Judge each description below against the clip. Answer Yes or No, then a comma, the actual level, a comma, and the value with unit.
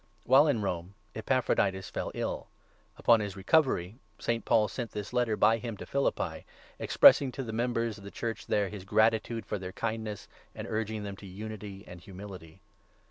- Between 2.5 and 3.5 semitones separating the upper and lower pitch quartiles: Yes, average, 2.8 semitones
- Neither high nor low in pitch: No, low, 110 Hz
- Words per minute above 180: No, average, 175 wpm